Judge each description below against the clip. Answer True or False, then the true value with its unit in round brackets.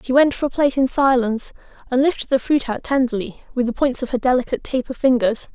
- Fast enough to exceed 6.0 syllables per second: True (6.4 syllables/s)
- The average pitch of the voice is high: True (260 Hz)